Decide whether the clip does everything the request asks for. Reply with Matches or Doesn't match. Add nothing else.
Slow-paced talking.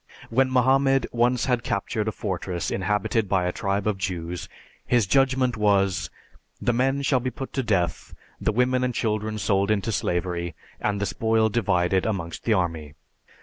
Doesn't match